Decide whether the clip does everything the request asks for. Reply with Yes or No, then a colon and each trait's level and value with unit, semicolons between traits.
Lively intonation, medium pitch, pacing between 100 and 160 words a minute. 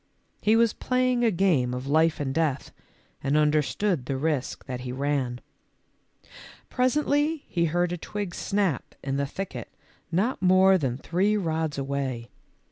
Yes: wide, 6.5 semitones; medium, 160 Hz; average, 145 wpm